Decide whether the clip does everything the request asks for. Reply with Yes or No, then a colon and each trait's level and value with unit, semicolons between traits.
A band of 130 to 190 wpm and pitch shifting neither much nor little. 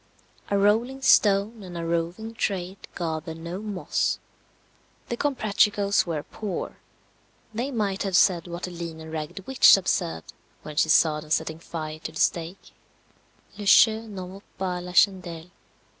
Yes: average, 155 wpm; average, 3.8 semitones